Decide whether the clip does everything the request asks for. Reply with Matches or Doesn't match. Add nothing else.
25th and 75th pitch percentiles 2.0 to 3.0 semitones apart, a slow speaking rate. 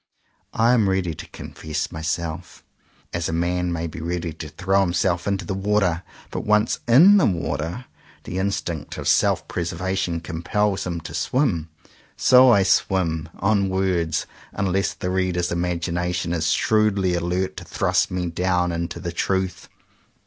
Doesn't match